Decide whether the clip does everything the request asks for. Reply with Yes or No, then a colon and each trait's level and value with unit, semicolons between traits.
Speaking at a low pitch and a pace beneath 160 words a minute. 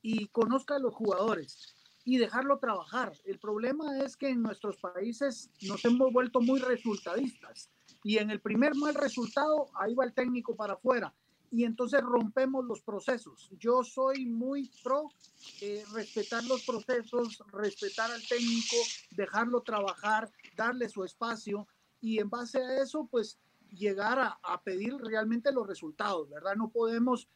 No: high, 235 Hz; average, 150 wpm